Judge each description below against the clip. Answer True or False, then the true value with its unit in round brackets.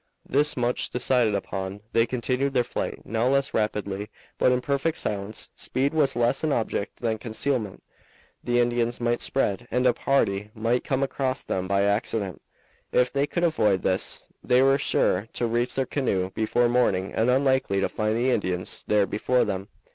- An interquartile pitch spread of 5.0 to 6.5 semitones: False (4.1 semitones)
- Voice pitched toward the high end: False (120 Hz)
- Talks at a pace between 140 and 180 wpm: True (175 wpm)